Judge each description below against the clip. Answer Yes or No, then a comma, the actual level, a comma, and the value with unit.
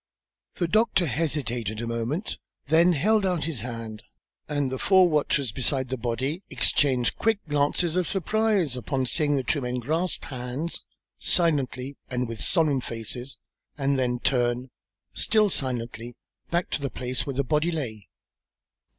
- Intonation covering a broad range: No, average, 5.0 semitones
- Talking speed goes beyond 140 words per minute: Yes, average, 150 wpm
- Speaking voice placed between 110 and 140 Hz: Yes, low, 135 Hz